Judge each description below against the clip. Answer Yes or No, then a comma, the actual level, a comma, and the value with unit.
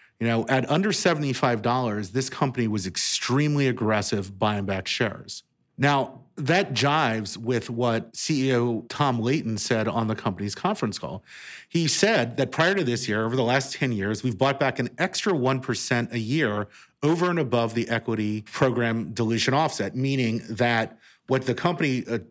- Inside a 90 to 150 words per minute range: No, average, 170 wpm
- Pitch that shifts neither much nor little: Yes, average, 3.3 semitones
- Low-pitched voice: Yes, low, 120 Hz